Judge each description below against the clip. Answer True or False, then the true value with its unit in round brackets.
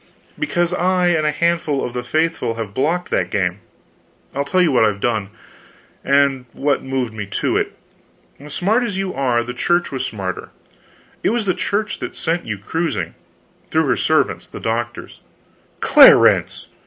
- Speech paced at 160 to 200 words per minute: True (165 wpm)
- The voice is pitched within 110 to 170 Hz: True (140 Hz)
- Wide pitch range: True (7.0 semitones)